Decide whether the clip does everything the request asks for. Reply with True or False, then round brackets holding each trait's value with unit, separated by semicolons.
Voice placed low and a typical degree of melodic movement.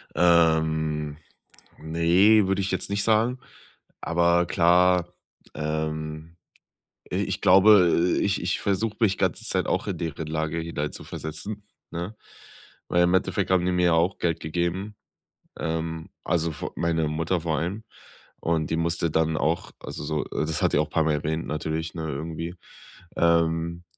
False (85 Hz; 2.3 semitones)